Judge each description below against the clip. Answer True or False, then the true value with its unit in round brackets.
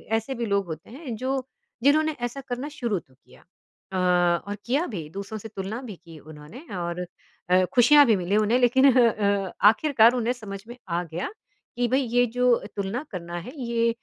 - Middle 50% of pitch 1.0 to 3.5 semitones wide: False (4.8 semitones)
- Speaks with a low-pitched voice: False (225 Hz)